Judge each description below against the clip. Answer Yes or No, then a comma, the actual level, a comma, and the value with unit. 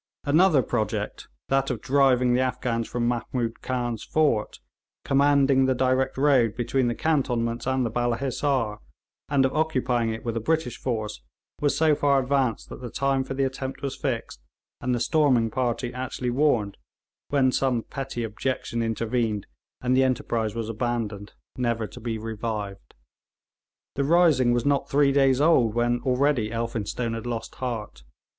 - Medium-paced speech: Yes, average, 160 wpm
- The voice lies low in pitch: Yes, low, 125 Hz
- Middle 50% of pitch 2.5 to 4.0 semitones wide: Yes, average, 2.8 semitones